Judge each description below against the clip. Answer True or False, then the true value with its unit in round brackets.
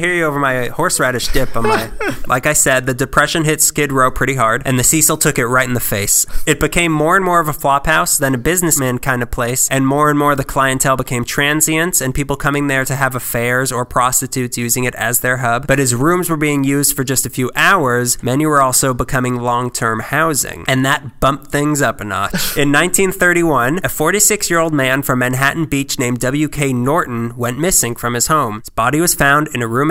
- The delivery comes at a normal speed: False (225 wpm)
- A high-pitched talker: False (135 Hz)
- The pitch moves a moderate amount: True (3.4 semitones)